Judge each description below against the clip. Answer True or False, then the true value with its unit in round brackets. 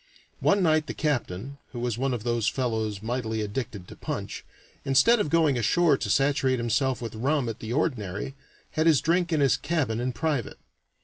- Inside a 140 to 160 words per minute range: False (185 wpm)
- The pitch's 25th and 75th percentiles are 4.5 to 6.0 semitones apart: True (5.0 semitones)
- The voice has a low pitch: True (130 Hz)